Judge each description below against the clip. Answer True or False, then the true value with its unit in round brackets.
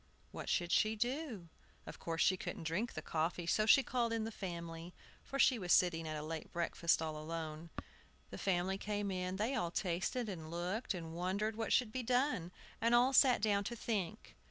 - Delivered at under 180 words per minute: False (200 wpm)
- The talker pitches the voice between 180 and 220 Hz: True (190 Hz)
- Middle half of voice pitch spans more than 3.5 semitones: True (5.0 semitones)